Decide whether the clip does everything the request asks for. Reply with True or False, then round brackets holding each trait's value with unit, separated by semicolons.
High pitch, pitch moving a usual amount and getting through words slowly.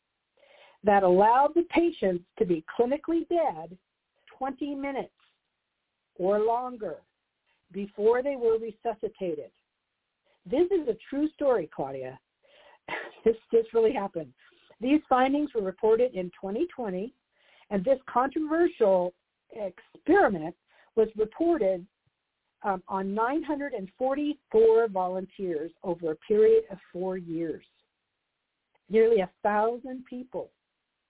False (225 Hz; 6.6 semitones; 100 wpm)